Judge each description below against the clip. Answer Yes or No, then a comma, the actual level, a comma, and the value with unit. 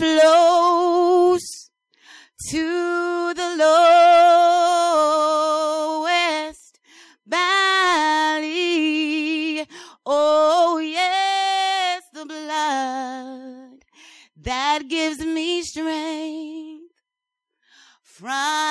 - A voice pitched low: No, very high, 320 Hz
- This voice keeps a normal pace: No, slow, 50 wpm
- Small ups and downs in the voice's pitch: Yes, narrow, 2.1 semitones